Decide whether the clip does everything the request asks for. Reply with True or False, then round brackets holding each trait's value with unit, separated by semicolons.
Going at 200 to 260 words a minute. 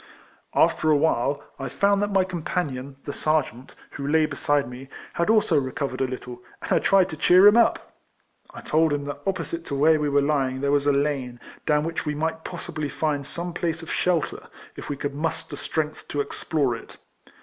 True (205 wpm)